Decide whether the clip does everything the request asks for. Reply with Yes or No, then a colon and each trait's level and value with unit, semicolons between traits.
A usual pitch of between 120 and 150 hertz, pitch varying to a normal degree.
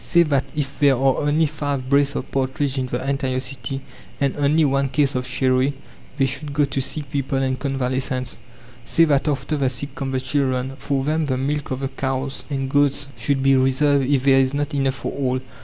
No: low, 135 Hz; narrow, 1.5 semitones